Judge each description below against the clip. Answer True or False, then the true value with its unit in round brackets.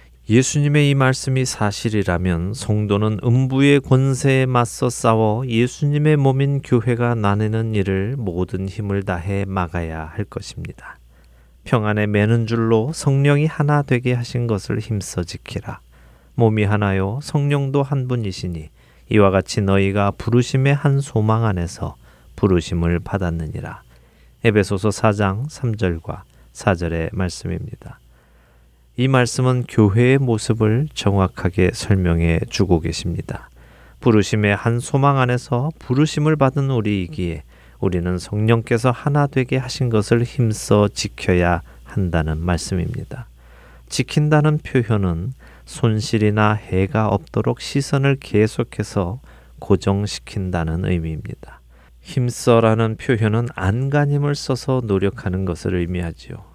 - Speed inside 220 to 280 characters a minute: True (275 characters per minute)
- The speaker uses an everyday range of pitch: False (5.7 semitones)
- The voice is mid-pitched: False (105 Hz)